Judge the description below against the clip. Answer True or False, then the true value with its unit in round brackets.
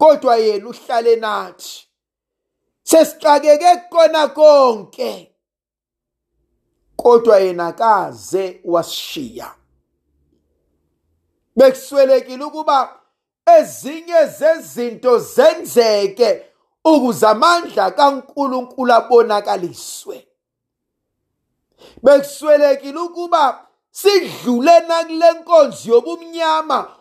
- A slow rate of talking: True (60 wpm)